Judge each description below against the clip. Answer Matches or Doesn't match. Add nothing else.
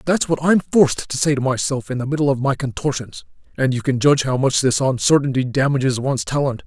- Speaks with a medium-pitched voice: Doesn't match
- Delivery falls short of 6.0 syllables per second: Doesn't match